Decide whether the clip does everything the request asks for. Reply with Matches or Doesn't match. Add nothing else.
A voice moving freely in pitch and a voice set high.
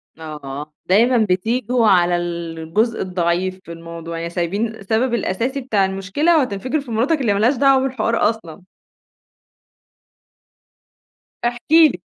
Matches